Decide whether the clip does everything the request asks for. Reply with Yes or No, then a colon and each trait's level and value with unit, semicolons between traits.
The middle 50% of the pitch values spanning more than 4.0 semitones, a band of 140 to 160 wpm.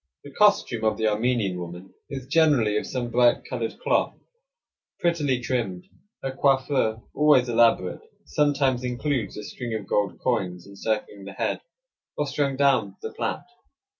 Yes: average, 4.4 semitones; average, 145 wpm